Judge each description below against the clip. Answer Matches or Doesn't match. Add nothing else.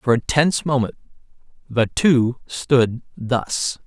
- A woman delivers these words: Doesn't match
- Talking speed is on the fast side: Doesn't match